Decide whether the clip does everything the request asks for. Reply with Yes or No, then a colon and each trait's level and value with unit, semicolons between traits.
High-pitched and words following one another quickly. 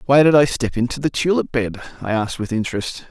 No: low, 130 Hz; fast, 230 wpm